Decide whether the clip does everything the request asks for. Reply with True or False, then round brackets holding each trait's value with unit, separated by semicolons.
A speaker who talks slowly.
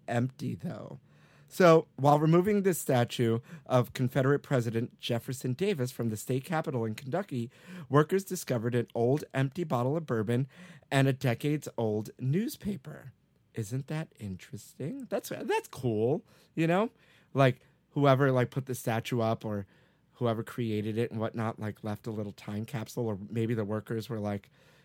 False (150 wpm)